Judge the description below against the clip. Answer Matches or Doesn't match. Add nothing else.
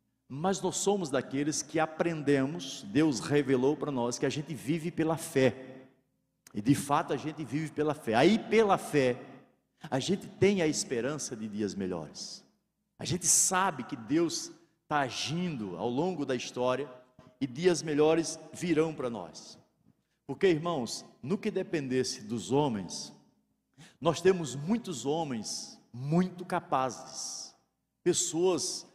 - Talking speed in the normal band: Matches